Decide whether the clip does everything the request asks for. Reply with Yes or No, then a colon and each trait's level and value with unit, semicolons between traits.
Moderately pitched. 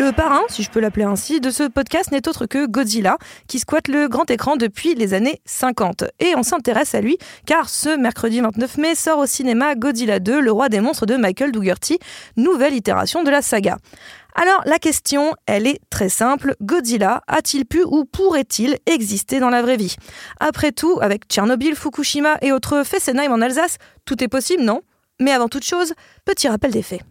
No: very high, 275 Hz